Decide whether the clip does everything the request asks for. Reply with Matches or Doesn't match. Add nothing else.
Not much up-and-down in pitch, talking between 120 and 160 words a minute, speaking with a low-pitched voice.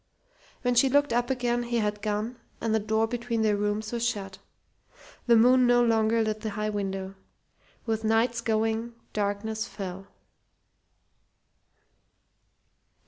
Doesn't match